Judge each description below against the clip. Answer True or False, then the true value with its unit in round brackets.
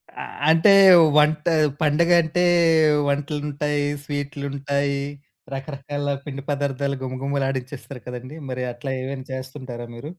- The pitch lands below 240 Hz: True (140 Hz)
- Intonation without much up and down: True (1.8 semitones)